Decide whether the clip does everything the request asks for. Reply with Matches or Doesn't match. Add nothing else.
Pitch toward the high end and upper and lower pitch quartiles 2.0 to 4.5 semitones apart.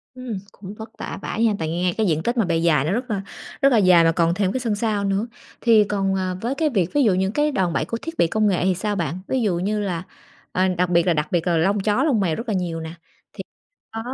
Matches